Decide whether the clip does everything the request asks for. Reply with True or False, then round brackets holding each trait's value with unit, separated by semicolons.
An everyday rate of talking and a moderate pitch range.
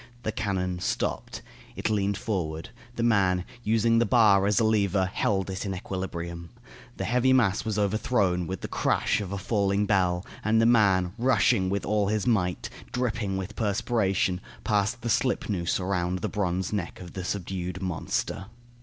True (165 wpm; 3.0 semitones)